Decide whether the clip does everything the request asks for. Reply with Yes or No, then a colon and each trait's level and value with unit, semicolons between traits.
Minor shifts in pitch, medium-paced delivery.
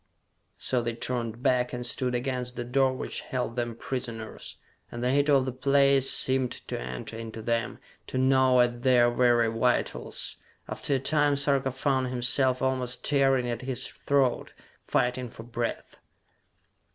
Yes: narrow, 1.7 semitones; average, 155 wpm